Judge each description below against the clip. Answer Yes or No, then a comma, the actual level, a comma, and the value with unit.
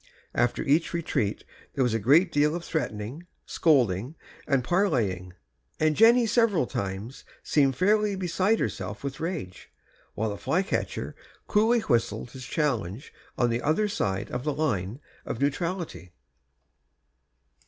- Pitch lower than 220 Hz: Yes, medium, 140 Hz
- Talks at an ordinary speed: No, slow, 130 wpm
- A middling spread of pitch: No, wide, 7.6 semitones